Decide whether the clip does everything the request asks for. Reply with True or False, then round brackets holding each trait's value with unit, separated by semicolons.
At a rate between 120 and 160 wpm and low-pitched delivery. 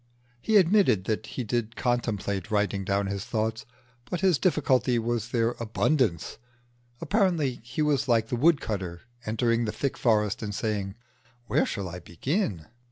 True (150 wpm; 115 Hz)